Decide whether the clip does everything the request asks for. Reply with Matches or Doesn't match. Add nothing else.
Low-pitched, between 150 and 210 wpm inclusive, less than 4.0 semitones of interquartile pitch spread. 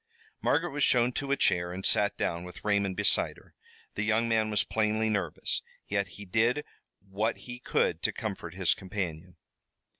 Matches